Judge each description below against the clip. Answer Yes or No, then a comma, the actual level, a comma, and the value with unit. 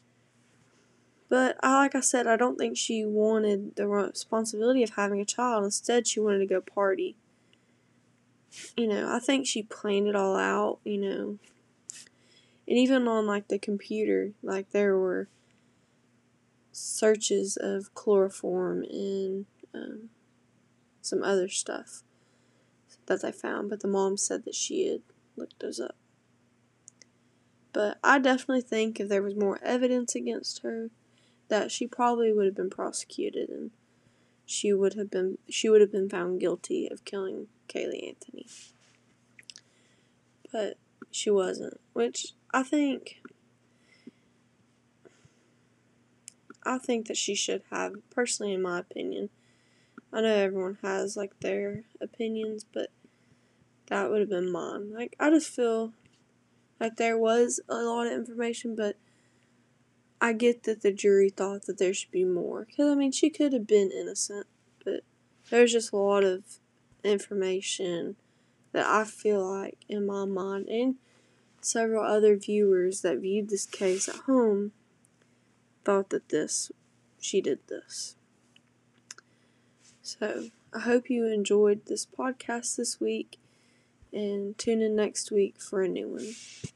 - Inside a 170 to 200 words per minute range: No, average, 140 wpm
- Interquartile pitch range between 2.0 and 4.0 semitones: Yes, average, 3.4 semitones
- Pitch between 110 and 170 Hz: No, high, 210 Hz